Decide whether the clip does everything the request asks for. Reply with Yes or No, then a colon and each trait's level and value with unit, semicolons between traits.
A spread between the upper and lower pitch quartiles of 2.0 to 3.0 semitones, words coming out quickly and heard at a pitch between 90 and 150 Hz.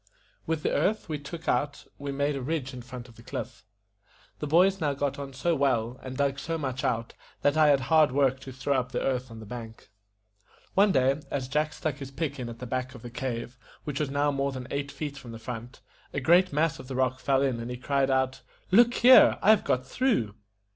Yes: average, 2.7 semitones; fast, 235 wpm; low, 135 Hz